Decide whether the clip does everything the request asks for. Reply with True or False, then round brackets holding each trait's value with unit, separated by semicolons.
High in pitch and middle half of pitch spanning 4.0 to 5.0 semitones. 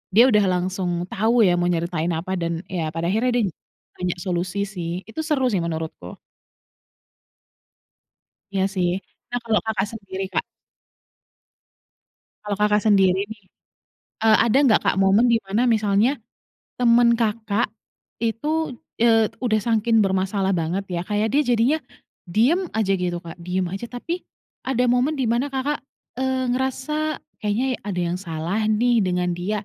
True (210 Hz; 4.5 semitones)